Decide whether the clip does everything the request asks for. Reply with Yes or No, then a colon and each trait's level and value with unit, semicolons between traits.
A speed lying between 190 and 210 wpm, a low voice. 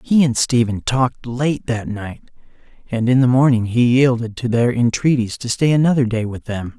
Yes: average, 195 wpm; low, 120 Hz